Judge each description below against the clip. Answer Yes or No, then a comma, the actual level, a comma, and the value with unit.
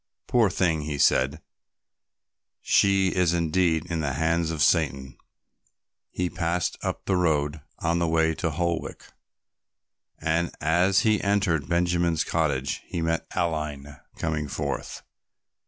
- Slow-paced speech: Yes, slow, 125 wpm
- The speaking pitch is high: No, very low, 80 Hz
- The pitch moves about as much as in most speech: No, narrow, 2.3 semitones